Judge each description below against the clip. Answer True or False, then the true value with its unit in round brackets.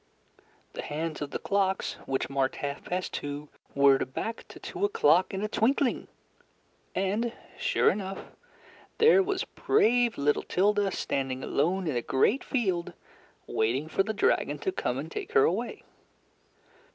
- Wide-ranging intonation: True (8.3 semitones)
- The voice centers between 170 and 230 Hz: True (190 Hz)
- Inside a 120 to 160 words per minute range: True (150 wpm)